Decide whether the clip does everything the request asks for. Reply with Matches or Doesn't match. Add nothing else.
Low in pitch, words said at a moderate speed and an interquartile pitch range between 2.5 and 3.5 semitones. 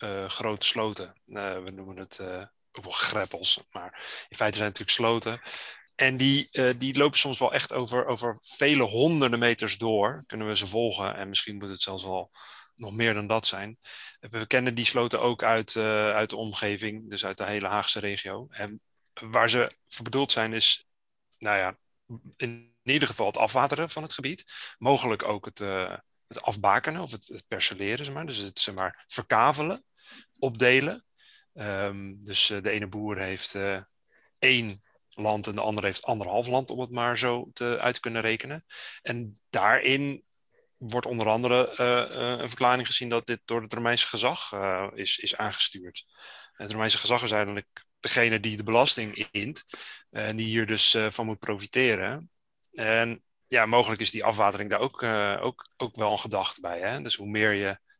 Matches